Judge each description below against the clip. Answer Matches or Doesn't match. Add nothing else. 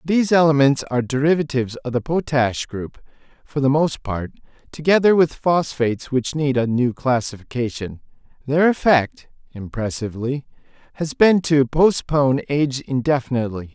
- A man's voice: Matches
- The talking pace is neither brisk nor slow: Doesn't match